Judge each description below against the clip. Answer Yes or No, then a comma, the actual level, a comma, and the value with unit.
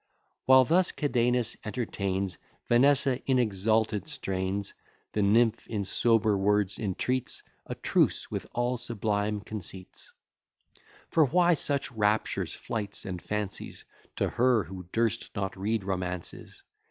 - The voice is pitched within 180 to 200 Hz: No, low, 110 Hz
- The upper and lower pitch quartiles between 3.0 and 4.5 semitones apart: Yes, average, 3.8 semitones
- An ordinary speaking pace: No, slow, 120 wpm